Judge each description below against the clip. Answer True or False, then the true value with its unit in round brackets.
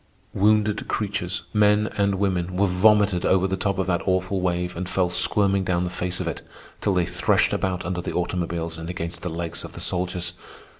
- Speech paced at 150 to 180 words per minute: False (200 wpm)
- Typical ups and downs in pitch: False (2.0 semitones)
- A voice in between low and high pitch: False (90 Hz)